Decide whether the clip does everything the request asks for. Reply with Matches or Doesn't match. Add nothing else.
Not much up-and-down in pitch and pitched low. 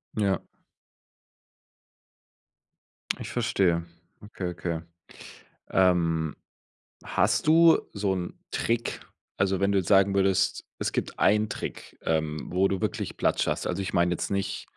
Matches